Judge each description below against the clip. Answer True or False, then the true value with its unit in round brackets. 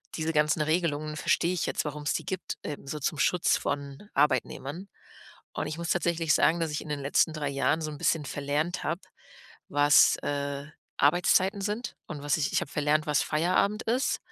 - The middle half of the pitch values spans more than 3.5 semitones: False (2.8 semitones)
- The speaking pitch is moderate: True (150 Hz)